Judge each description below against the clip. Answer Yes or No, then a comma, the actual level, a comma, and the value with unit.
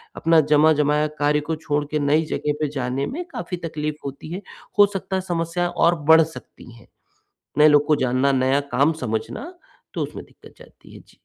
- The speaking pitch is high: No, medium, 150 Hz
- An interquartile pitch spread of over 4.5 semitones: No, average, 2.7 semitones